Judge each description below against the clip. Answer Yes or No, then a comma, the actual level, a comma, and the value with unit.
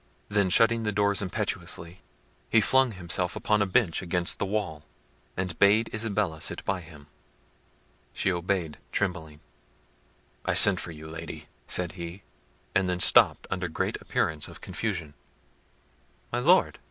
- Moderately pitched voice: No, very low, 90 Hz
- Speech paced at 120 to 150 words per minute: Yes, average, 140 wpm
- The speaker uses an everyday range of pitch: Yes, average, 3.7 semitones